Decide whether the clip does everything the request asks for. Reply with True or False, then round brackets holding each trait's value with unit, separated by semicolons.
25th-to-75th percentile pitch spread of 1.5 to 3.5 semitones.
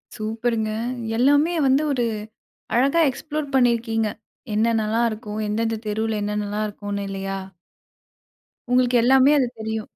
True (3.0 semitones)